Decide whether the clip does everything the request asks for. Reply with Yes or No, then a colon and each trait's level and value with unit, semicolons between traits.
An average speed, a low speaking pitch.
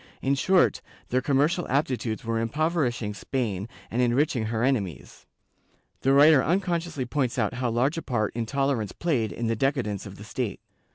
Yes: average, 165 wpm; low, 125 Hz